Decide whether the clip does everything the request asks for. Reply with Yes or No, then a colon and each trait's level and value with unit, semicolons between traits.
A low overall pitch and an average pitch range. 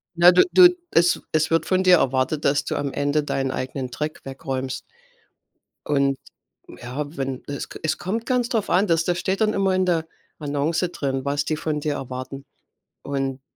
No: medium, 150 Hz; average, 4.6 semitones